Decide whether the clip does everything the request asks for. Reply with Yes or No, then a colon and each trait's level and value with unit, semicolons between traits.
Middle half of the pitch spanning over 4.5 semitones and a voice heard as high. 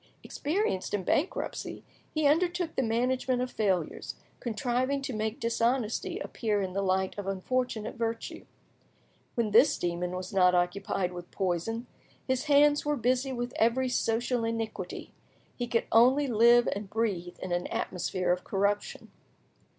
Yes: average, 5.0 semitones; high, 230 Hz